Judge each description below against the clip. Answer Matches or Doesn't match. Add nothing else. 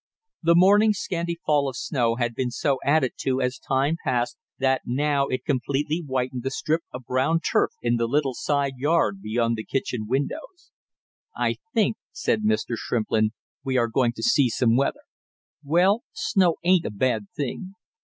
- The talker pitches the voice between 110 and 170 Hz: Matches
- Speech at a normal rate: Matches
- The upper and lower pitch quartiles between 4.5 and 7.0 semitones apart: Matches